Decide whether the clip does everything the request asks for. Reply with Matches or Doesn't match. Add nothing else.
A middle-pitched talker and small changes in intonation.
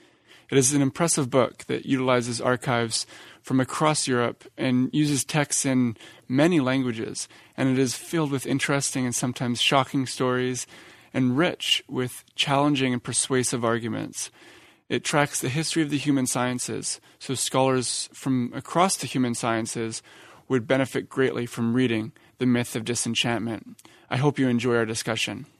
Doesn't match